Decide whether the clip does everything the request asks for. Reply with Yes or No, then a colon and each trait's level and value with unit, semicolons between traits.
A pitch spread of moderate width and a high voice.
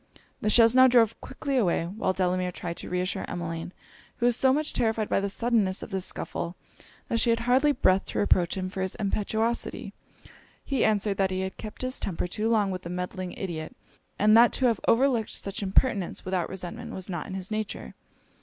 Yes: average, 3.9 semitones; high, 200 Hz